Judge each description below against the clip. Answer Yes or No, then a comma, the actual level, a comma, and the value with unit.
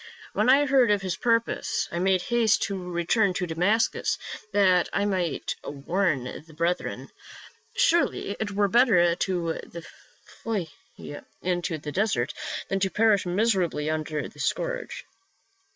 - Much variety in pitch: No, average, 4.3 semitones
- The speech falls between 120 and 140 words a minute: Yes, slow, 135 wpm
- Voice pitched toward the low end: No, high, 190 Hz